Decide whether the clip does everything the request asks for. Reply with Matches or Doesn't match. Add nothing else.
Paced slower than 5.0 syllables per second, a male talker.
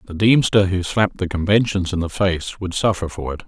Doesn't match